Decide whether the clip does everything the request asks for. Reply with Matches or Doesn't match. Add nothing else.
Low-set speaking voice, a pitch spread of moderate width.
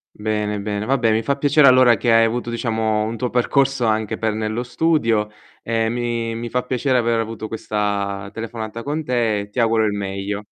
Doesn't match